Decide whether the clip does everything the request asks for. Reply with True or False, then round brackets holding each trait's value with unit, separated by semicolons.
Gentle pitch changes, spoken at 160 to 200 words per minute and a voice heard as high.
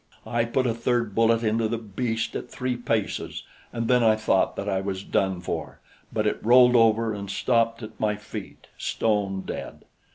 False (1.9 semitones; 185 wpm; 115 Hz)